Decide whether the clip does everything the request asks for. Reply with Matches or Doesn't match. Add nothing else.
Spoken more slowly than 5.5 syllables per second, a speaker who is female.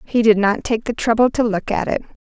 Doesn't match